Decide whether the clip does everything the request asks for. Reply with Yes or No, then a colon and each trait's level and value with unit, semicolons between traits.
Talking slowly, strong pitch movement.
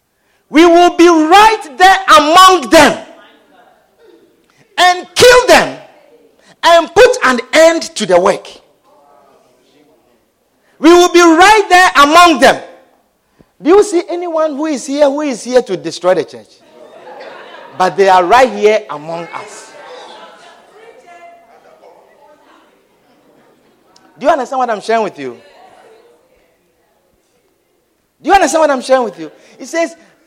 Yes: slow, 125 wpm; wide, 6.1 semitones